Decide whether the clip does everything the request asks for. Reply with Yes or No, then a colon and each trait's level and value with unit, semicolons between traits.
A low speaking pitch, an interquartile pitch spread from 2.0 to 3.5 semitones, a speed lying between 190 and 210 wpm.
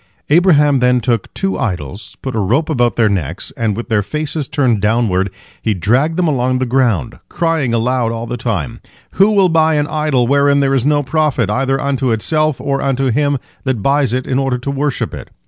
No: low, 130 Hz; average, 4.0 semitones; average, 200 wpm